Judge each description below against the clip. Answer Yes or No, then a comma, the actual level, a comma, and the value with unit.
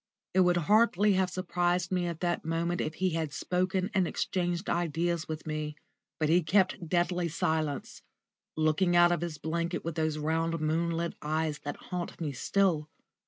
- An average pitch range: No, narrow, 2.2 semitones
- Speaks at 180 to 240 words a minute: No, average, 170 wpm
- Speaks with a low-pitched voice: No, medium, 170 Hz